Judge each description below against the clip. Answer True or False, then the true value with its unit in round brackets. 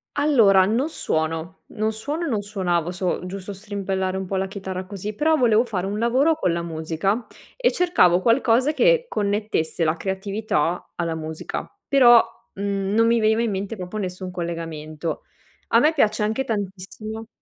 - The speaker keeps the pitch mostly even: False (4.0 semitones)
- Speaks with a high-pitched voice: True (200 Hz)